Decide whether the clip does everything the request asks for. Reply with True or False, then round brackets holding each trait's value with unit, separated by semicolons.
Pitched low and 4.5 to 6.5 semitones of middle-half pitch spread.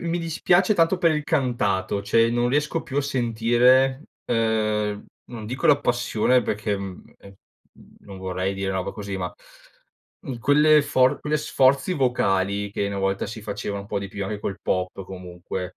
True (110 Hz; 5.4 semitones)